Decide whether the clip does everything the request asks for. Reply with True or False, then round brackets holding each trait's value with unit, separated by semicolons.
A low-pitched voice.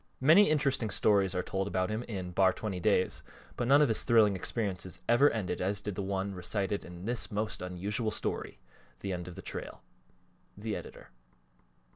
True (100 Hz)